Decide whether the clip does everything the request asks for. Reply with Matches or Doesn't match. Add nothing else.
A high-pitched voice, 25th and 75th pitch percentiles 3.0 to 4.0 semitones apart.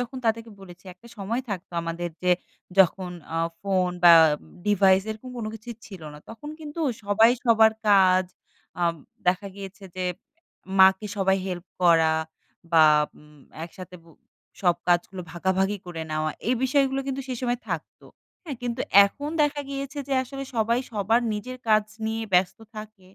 Doesn't match